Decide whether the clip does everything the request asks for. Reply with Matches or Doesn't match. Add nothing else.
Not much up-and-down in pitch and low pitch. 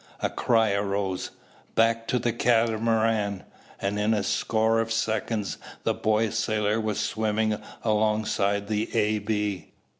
Matches